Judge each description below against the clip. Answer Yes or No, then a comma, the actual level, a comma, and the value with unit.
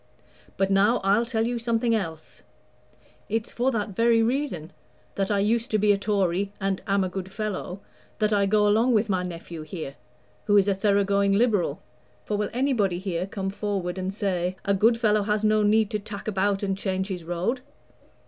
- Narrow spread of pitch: Yes, narrow, 2.3 semitones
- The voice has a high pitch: Yes, high, 200 Hz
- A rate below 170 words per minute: No, average, 195 wpm